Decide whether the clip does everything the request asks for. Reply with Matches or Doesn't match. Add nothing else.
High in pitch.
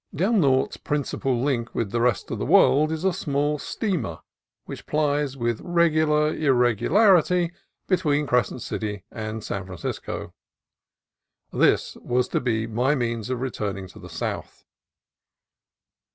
Doesn't match